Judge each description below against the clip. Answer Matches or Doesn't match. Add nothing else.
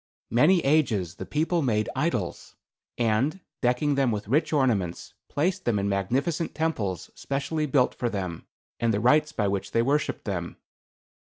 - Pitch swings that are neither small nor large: Doesn't match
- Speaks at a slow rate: Doesn't match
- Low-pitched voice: Matches